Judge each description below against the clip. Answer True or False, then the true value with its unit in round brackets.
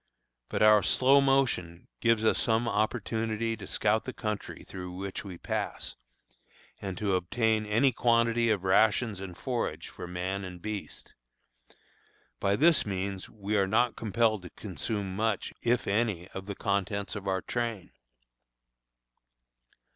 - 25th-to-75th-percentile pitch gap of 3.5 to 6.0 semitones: False (3.1 semitones)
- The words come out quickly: False (140 wpm)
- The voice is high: False (105 Hz)